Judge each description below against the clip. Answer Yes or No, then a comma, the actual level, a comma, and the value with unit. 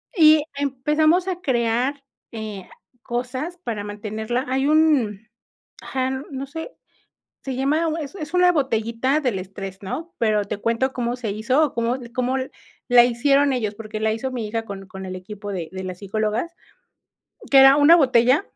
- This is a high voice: Yes, high, 245 Hz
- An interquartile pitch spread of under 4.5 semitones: No, average, 4.8 semitones